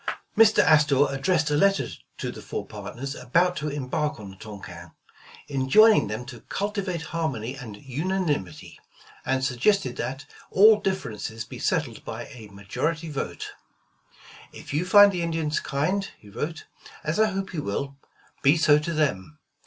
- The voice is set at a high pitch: No, medium, 150 Hz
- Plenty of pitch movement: Yes, wide, 6.1 semitones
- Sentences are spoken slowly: No, average, 155 wpm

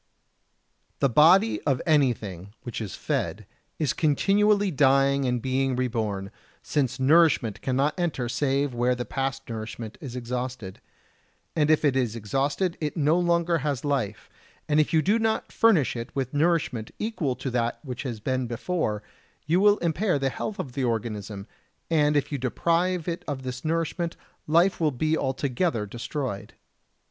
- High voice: No, low, 135 Hz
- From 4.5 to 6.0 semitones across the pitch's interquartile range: Yes, average, 4.9 semitones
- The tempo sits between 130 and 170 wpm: Yes, average, 160 wpm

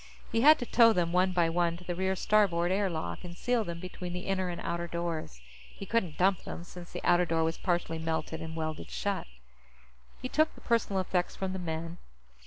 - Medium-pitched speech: Yes, medium, 175 Hz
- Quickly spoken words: Yes, fast, 215 wpm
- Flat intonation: Yes, narrow, 2.3 semitones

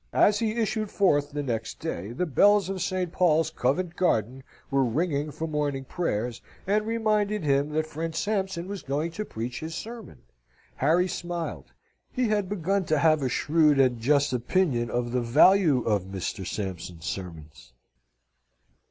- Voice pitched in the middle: Yes, medium, 155 Hz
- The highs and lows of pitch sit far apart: Yes, wide, 7.0 semitones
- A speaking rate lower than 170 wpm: Yes, average, 160 wpm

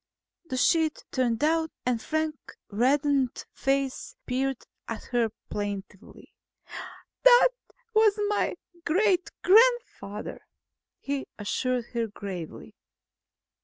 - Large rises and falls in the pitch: Yes, wide, 6.0 semitones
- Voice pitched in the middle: No, very high, 270 Hz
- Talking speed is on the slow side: Yes, slow, 90 wpm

